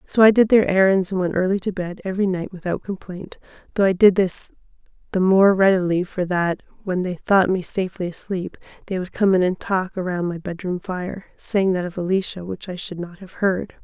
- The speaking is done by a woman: Yes, female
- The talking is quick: Yes, fast, 210 wpm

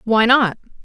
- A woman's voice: Yes, female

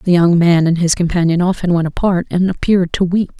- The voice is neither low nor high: Yes, medium, 175 Hz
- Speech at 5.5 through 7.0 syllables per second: Yes, 5.9 syllables/s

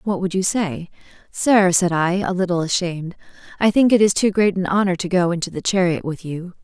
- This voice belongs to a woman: Yes, female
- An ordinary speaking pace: No, fast, 215 wpm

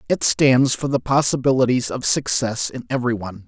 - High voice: No, low, 125 Hz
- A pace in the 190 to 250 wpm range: No, average, 170 wpm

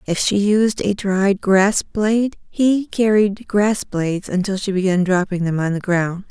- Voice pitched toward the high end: Yes, high, 200 Hz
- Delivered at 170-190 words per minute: Yes, average, 180 wpm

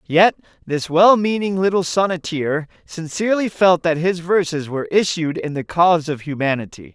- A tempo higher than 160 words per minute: No, average, 155 wpm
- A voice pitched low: No, medium, 170 Hz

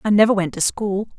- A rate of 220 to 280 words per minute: Yes, fast, 255 wpm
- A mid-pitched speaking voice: No, high, 200 Hz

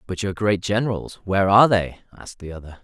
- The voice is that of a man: Yes, male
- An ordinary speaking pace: Yes, average, 190 wpm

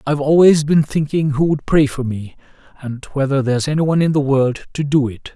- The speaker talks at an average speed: No, fast, 225 wpm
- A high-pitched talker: No, medium, 140 Hz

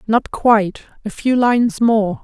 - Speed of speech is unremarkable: Yes, average, 160 wpm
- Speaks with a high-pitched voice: Yes, high, 225 Hz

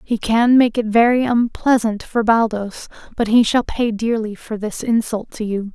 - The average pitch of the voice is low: No, high, 225 Hz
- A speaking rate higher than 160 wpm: Yes, average, 190 wpm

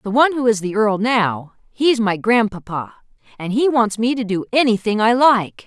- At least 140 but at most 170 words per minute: No, average, 200 wpm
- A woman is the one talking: Yes, female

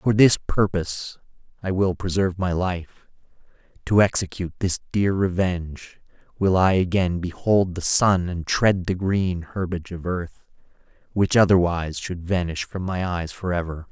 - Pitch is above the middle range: No, very low, 90 Hz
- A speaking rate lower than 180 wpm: Yes, average, 145 wpm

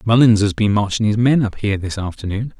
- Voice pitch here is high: No, low, 105 Hz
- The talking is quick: Yes, fast, 230 wpm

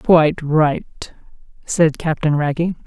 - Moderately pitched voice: Yes, medium, 155 Hz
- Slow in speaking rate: Yes, slow, 105 wpm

